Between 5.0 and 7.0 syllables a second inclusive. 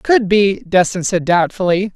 No: 4.3 syllables/s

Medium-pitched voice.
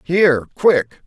Yes: medium, 160 Hz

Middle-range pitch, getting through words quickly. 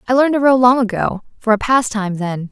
No: high, 230 Hz; fast, 215 wpm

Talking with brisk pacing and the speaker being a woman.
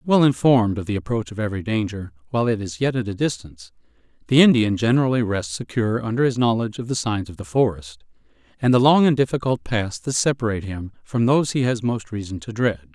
No: fast, 215 wpm; male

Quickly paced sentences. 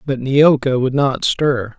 No: average, 170 wpm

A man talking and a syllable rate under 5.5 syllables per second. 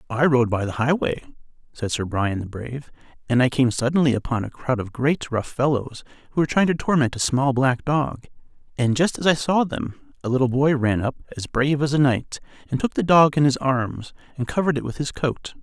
No: male; 5.6 syllables/s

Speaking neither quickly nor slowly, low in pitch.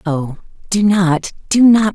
No: average, 155 wpm; high, 190 Hz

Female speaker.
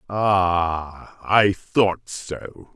No: male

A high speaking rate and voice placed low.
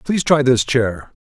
No: average, 195 wpm; low, 125 Hz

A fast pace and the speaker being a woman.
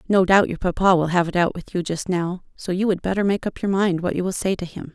Yes: fast, 315 wpm; female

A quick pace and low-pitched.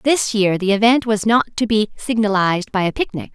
No: fast, 215 wpm; high, 215 Hz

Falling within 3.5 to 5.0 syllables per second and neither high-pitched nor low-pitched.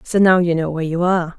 No: 7.0 syllables/s; medium, 175 Hz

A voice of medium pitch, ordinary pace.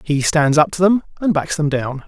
No: medium, 155 Hz; fast, 260 wpm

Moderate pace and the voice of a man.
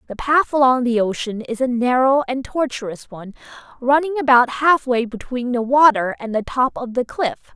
No: average, 185 wpm; female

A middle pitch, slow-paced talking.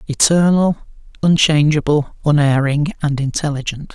Yes: medium, 150 Hz; slow, 75 wpm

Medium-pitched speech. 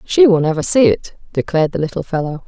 Yes: medium, 175 Hz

